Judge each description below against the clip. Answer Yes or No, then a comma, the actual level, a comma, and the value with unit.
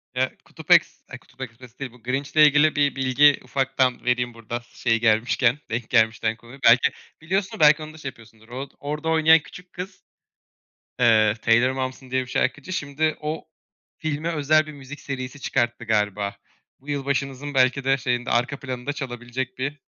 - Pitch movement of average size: Yes, average, 3.1 semitones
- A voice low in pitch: Yes, low, 130 Hz